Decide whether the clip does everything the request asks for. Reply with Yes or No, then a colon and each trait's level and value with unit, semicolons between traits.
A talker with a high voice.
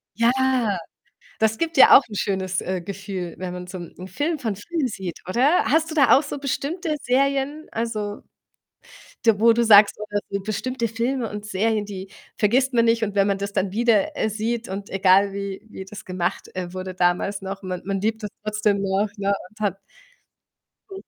Yes: high, 210 Hz